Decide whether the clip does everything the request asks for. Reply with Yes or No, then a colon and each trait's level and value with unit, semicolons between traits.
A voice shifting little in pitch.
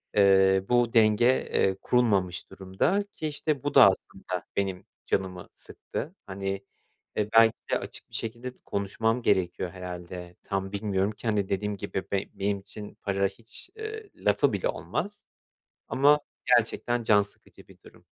No: average, 3.9 semitones